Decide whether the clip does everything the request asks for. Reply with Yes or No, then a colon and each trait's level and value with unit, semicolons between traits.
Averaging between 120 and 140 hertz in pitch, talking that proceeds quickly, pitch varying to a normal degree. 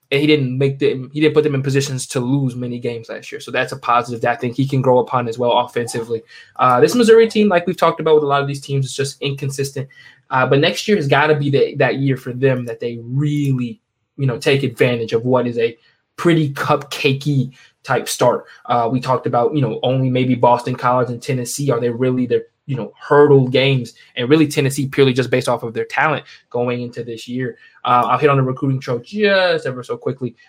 Yes: low, 135 Hz; fast, 240 wpm; average, 3.0 semitones